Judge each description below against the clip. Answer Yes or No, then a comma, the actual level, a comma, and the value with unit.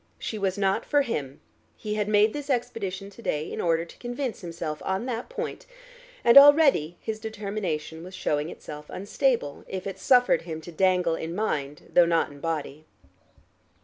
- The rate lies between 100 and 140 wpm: No, average, 175 wpm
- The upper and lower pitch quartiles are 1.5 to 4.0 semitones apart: No, wide, 5.4 semitones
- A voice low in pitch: No, high, 190 Hz